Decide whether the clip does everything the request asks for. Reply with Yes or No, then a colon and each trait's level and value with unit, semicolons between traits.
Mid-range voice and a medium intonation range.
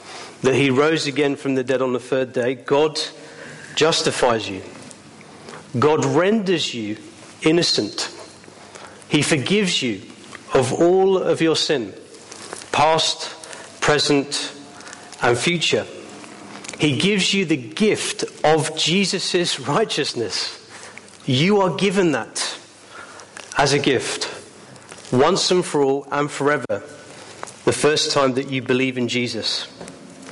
Yes: medium, 150 Hz; average, 5.0 semitones